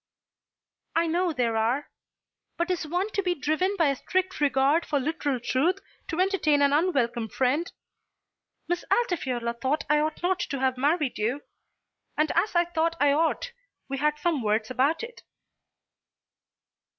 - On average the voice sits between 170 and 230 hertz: No, very high, 300 Hz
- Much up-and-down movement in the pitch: No, average, 4.8 semitones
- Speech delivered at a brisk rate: No, average, 160 wpm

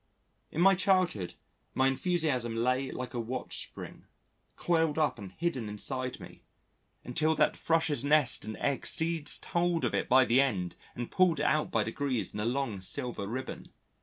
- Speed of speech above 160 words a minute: Yes, average, 170 wpm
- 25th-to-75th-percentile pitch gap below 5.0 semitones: No, wide, 5.5 semitones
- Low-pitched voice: Yes, low, 130 Hz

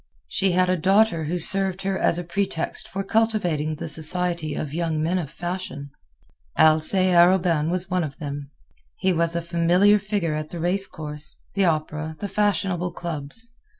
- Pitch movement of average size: Yes, average, 3.3 semitones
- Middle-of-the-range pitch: Yes, medium, 175 Hz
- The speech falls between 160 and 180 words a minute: Yes, average, 170 wpm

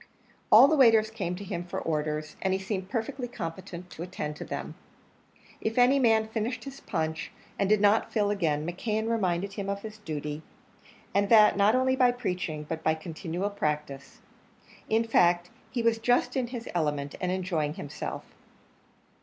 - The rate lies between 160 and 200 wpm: Yes, average, 170 wpm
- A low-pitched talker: No, high, 195 Hz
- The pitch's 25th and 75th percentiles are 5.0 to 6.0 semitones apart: Yes, wide, 5.5 semitones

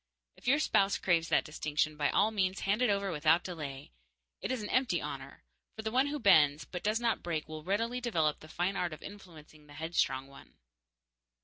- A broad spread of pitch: Yes, wide, 5.8 semitones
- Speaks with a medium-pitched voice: Yes, medium, 175 Hz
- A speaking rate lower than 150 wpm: No, fast, 205 wpm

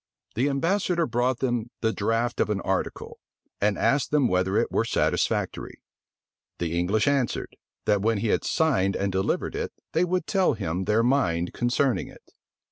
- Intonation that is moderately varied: No, wide, 6.0 semitones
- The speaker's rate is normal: Yes, average, 165 wpm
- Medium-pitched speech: No, low, 115 Hz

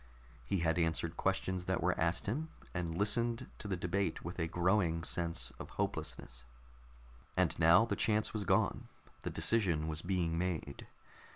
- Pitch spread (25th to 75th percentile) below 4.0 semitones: Yes, average, 3.1 semitones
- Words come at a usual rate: Yes, average, 160 wpm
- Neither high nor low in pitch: No, very low, 90 Hz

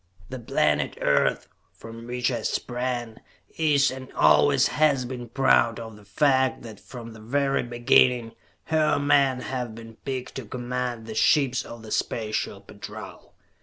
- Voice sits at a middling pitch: No, low, 125 Hz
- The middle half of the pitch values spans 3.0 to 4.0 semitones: No, narrow, 2.6 semitones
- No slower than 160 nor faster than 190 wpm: No, average, 150 wpm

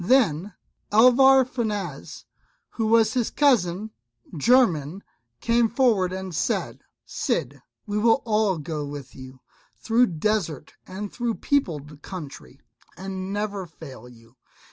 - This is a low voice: No, high, 195 Hz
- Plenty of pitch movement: Yes, wide, 6.7 semitones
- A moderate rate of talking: No, slow, 120 wpm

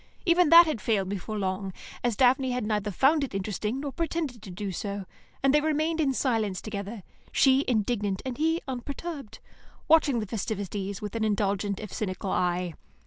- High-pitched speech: Yes, high, 220 Hz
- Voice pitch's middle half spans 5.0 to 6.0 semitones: Yes, wide, 5.5 semitones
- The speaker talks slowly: No, average, 175 wpm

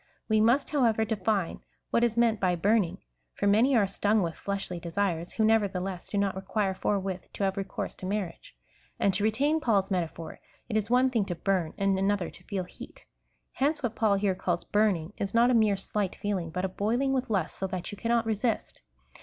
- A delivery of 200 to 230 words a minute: Yes, fast, 205 wpm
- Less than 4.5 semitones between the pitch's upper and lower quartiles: Yes, average, 2.9 semitones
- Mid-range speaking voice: No, high, 200 Hz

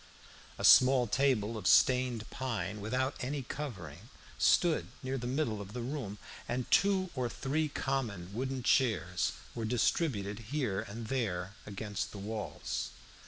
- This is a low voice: Yes, low, 120 Hz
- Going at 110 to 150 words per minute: Yes, average, 140 wpm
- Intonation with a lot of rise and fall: No, average, 4.4 semitones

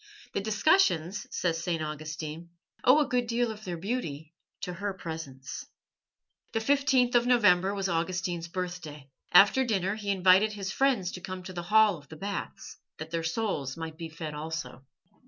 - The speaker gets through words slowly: No, average, 170 wpm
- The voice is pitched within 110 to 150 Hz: No, medium, 185 Hz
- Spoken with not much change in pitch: No, average, 4.8 semitones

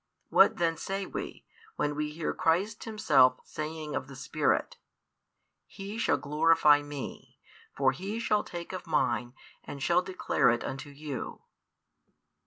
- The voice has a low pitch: No, medium, 155 Hz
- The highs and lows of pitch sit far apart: No, average, 4.6 semitones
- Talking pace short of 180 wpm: Yes, average, 140 wpm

